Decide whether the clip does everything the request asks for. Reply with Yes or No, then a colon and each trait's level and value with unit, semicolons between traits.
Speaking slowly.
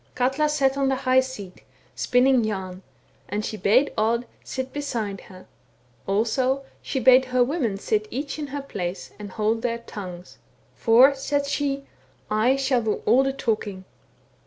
No: average, 170 wpm